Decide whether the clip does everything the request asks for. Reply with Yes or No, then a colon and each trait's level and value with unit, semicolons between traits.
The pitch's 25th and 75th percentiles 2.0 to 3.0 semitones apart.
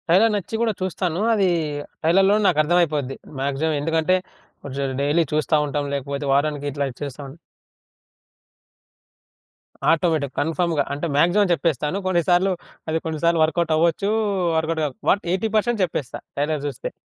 No: average, 3.5 semitones